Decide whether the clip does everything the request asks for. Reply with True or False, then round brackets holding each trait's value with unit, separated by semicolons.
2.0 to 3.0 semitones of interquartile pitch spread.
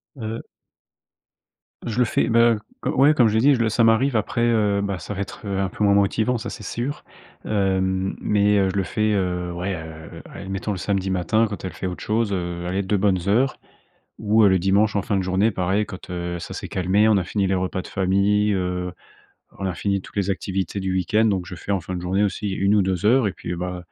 True (2.5 semitones)